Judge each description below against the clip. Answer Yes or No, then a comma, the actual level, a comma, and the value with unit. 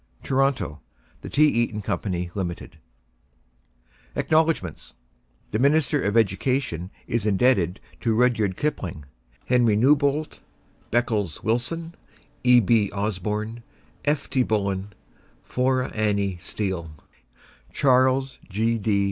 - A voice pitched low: Yes, low, 115 Hz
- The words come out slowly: Yes, slow, 100 wpm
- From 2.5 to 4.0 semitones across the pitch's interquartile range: No, average, 4.6 semitones